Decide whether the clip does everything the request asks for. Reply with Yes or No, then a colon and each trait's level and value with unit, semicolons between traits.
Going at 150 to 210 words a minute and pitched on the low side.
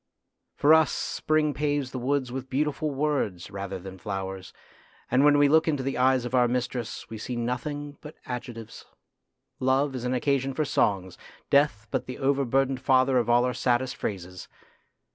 Yes: average, 170 wpm; low, 130 Hz